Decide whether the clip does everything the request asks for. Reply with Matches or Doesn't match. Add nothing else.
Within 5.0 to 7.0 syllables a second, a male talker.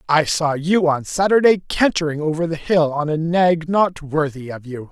Doesn't match